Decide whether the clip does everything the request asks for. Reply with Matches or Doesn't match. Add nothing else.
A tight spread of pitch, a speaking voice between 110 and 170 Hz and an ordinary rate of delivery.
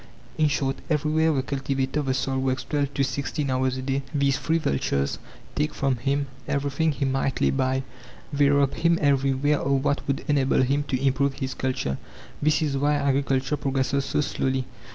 Matches